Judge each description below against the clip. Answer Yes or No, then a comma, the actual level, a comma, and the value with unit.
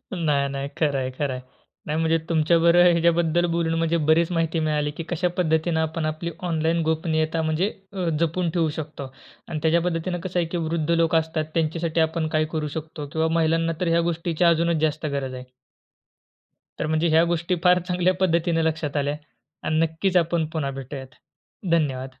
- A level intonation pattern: Yes, narrow, 1.4 semitones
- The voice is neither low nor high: Yes, medium, 160 Hz